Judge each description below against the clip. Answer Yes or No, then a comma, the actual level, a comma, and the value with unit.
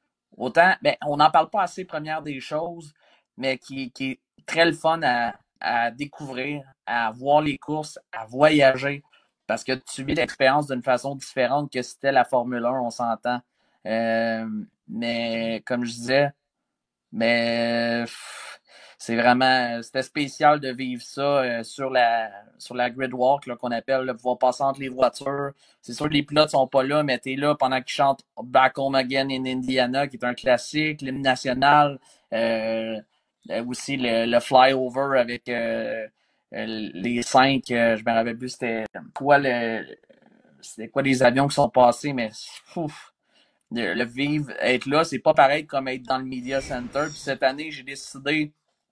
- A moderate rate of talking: Yes, average, 165 wpm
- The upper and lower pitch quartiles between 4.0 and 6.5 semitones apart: No, average, 2.8 semitones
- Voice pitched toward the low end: Yes, low, 130 Hz